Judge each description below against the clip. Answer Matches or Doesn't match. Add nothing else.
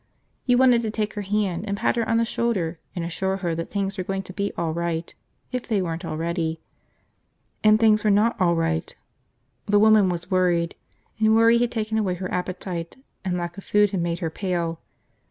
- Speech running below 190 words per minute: Doesn't match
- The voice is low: Doesn't match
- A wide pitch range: Doesn't match